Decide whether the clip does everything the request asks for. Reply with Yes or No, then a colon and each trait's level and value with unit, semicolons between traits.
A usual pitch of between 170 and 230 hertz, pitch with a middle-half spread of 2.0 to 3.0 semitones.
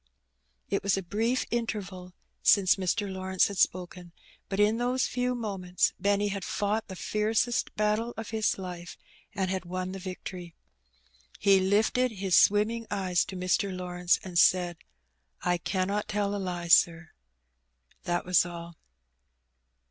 Yes: high, 190 Hz; narrow, 2.6 semitones